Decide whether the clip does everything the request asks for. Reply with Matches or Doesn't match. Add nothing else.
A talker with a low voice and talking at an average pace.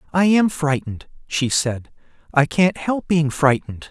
Doesn't match